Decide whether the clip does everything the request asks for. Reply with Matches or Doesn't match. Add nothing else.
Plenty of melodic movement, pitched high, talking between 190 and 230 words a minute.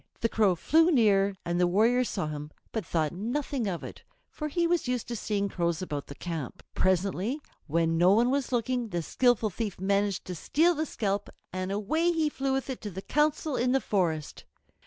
Matches